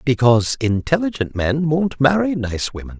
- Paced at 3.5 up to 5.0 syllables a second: Yes, 4.9 syllables/s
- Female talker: No, male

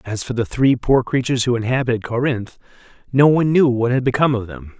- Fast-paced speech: Yes, fast, 215 wpm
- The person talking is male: Yes, male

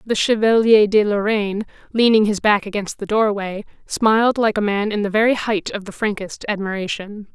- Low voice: No, high, 210 Hz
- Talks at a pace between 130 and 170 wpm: No, average, 180 wpm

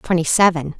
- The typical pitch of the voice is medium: Yes, medium, 170 Hz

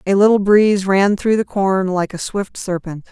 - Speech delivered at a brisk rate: Yes, fast, 210 wpm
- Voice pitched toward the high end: Yes, high, 195 Hz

